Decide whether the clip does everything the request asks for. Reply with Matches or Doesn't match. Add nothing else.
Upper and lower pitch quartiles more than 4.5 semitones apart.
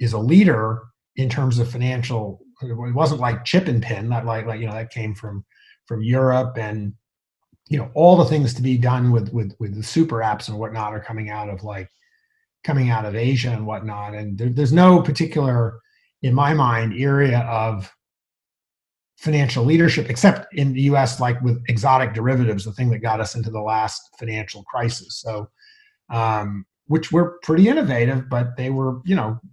Doesn't match